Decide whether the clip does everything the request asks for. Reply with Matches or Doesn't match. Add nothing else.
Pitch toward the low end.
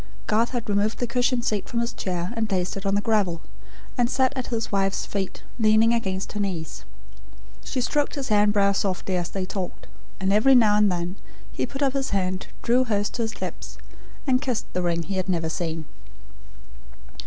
Doesn't match